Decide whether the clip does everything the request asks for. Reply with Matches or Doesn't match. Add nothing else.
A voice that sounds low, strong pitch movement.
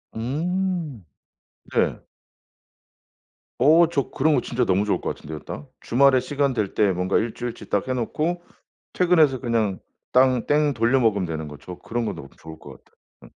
Matches